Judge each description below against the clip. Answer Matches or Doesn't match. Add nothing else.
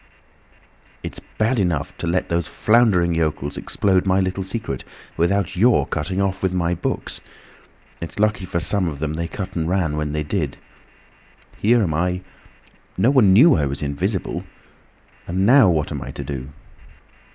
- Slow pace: Doesn't match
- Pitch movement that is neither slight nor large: Matches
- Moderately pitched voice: Doesn't match